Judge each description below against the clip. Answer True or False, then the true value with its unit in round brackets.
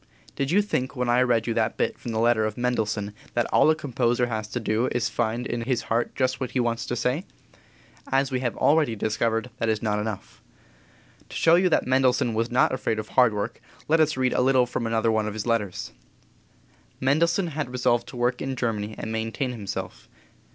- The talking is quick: True (215 wpm)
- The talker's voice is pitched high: False (120 Hz)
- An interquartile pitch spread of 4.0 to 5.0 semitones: False (2.6 semitones)